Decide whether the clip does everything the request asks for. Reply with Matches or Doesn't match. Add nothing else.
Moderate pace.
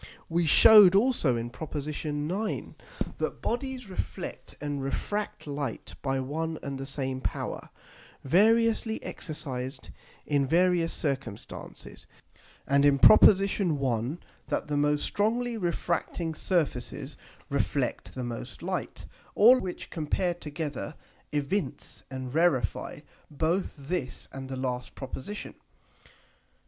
Doesn't match